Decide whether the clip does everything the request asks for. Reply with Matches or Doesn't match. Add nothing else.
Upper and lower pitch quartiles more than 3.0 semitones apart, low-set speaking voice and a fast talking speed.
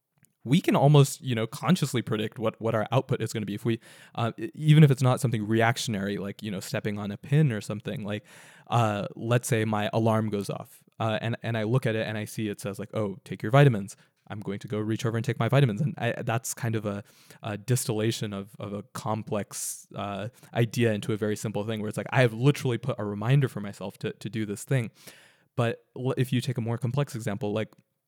Matches